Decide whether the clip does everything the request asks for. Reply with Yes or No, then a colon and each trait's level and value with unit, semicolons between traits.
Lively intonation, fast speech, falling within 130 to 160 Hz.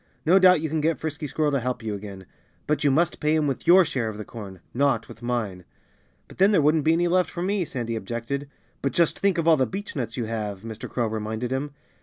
Yes: wide, 6.0 semitones; fast, 245 wpm; medium, 140 Hz